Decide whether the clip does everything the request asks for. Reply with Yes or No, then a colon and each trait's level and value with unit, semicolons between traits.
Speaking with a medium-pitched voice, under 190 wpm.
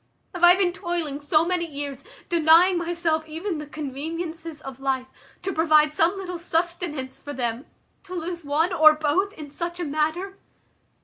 No: very high, 320 Hz; average, 165 wpm